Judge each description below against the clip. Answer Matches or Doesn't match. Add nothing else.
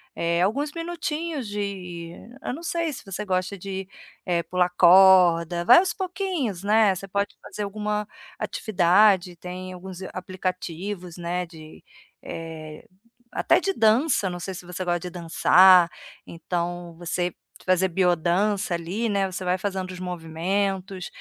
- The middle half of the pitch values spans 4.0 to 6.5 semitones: Doesn't match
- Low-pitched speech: Doesn't match